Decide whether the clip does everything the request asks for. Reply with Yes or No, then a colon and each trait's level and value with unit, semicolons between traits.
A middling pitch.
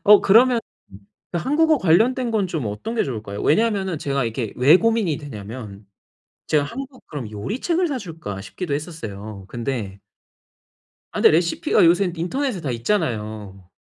Yes: medium, 160 Hz